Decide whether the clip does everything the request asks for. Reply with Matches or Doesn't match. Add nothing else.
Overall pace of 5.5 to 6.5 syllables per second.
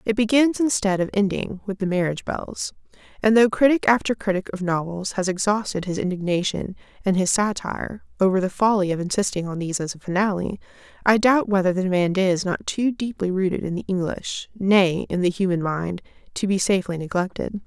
Matches